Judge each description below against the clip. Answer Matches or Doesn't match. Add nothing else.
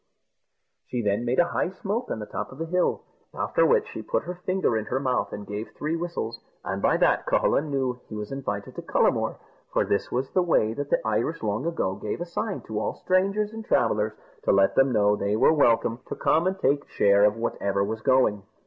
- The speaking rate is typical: Doesn't match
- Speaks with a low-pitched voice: Matches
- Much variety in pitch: Matches